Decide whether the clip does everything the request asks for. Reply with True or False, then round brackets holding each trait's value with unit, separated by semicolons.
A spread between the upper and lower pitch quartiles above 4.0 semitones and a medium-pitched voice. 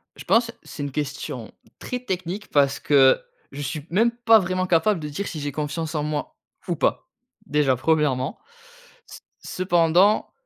True (4.4 semitones; 160 Hz)